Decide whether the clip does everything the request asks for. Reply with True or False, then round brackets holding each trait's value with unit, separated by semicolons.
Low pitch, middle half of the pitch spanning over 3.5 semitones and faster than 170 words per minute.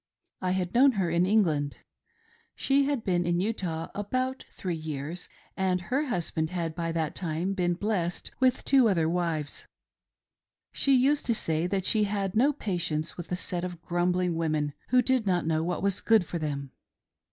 False (180 Hz; 4.5 semitones; 180 wpm)